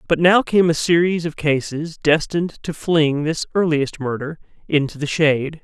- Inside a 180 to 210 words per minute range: No, average, 170 wpm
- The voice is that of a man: Yes, male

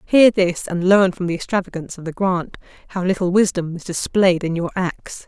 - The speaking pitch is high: No, medium, 180 Hz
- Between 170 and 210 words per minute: Yes, fast, 205 wpm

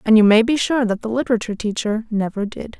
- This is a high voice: Yes, high, 225 Hz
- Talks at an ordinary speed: No, fast, 235 wpm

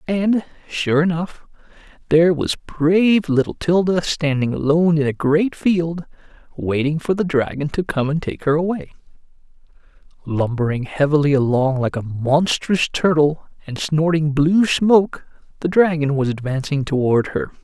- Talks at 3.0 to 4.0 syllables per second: No, 4.6 syllables/s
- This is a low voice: No, medium, 155 Hz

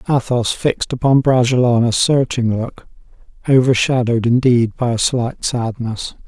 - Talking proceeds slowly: Yes, slow, 125 wpm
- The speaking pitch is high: No, low, 120 Hz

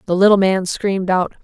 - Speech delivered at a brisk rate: Yes, fast, 210 wpm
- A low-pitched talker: No, high, 190 Hz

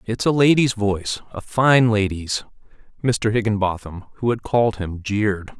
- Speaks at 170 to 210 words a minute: No, average, 150 wpm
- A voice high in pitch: No, low, 110 Hz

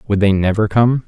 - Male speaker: Yes, male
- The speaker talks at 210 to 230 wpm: Yes, fast, 225 wpm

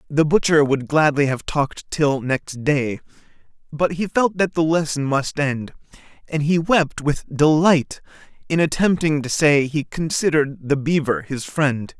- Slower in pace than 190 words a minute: Yes, average, 160 wpm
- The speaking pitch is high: No, medium, 150 Hz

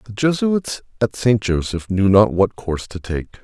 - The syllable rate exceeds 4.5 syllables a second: Yes, 4.8 syllables/s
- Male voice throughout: Yes, male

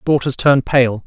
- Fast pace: No, average, 170 wpm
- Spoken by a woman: No, male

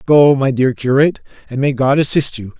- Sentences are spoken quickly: Yes, fast, 210 wpm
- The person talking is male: Yes, male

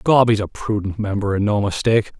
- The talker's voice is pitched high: No, low, 105 Hz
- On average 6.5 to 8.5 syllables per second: No, 5.9 syllables/s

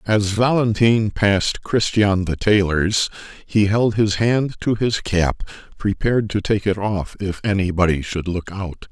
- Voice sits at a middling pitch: No, low, 100 Hz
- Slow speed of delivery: No, average, 155 wpm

